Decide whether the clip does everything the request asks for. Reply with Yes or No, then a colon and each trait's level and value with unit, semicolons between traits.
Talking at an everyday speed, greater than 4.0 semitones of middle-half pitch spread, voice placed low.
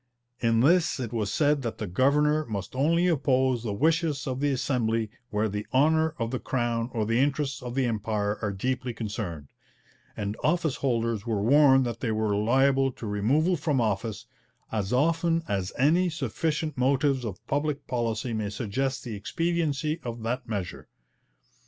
Yes: average, 165 wpm; average, 4.8 semitones; low, 125 Hz